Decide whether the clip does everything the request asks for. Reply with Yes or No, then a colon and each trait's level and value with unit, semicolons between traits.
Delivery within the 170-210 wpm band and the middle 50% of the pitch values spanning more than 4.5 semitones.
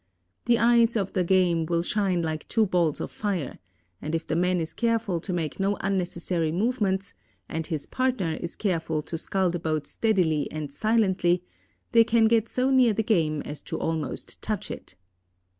Yes: average, 180 wpm; average, 5.1 semitones